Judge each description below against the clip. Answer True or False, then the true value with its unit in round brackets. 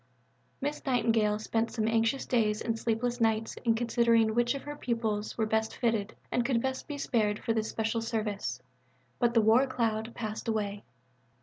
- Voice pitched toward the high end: True (225 Hz)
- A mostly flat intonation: True (1.7 semitones)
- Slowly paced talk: False (175 wpm)